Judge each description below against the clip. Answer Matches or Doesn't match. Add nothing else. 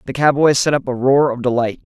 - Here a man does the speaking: Matches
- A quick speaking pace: Matches